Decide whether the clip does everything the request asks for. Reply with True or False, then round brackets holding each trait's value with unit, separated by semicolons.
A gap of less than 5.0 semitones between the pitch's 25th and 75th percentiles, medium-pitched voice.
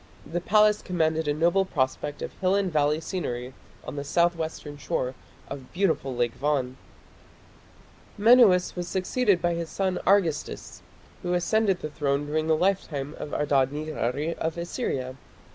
True (4.1 semitones; 160 Hz)